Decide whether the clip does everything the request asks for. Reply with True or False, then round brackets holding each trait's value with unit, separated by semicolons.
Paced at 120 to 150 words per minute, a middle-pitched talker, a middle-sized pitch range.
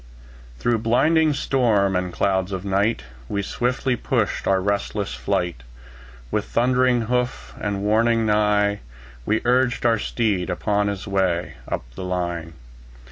False (135 wpm; 105 Hz; 3.8 semitones)